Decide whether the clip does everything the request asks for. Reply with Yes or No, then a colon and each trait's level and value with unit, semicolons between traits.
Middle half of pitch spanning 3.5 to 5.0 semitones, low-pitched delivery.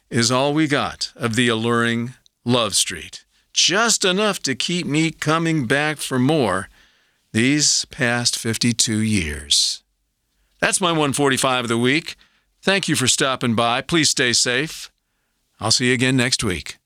Yes: average, 4.5 semitones; low, 130 Hz